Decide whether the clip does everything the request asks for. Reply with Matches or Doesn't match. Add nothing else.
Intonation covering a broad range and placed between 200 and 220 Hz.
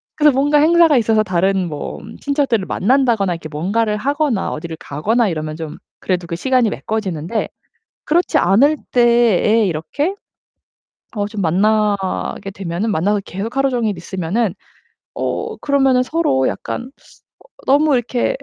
Matches